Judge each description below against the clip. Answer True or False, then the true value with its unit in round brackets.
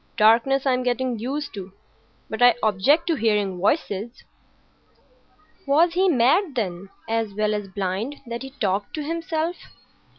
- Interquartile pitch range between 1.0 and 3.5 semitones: False (5.6 semitones)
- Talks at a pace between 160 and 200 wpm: False (140 wpm)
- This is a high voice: True (235 Hz)